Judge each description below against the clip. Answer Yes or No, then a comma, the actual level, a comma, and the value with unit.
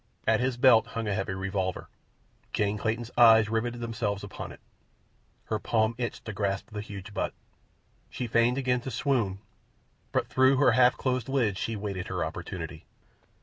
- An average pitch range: Yes, average, 3.2 semitones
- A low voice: Yes, low, 110 Hz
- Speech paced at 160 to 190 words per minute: Yes, average, 165 wpm